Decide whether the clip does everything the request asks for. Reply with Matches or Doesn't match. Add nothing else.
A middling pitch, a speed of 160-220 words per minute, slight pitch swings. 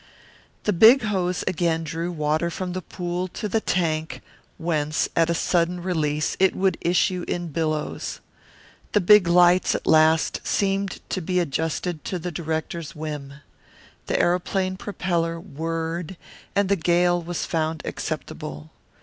Doesn't match